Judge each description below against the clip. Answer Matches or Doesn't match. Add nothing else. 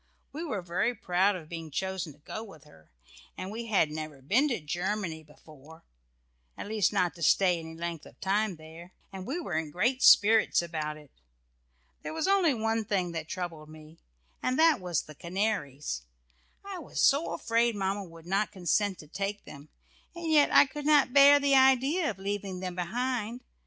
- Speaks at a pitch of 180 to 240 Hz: Matches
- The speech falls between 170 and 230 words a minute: Matches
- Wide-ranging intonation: Matches